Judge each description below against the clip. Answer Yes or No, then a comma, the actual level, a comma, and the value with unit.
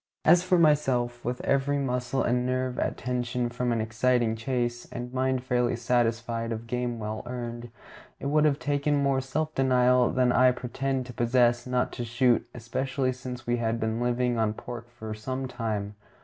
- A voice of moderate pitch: No, low, 125 Hz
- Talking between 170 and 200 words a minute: Yes, average, 175 wpm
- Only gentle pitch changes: Yes, narrow, 1.6 semitones